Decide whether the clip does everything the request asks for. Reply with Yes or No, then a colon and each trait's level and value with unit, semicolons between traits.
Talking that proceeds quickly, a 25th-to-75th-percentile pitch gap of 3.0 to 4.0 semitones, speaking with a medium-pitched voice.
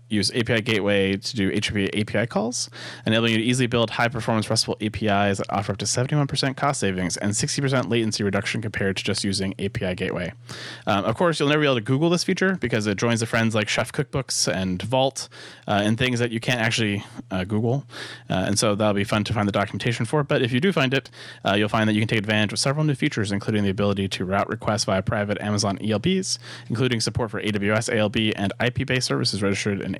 No: fast, 230 wpm; average, 3.4 semitones; low, 110 Hz